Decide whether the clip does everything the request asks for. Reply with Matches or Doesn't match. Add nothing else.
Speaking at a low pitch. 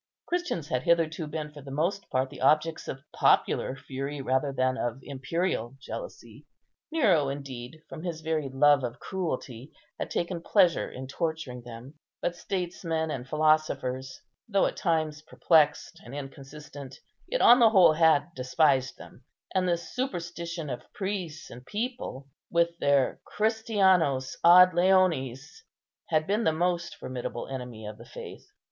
Doesn't match